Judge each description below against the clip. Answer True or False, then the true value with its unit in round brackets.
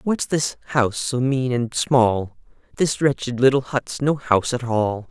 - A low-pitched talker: True (125 Hz)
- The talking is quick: False (175 wpm)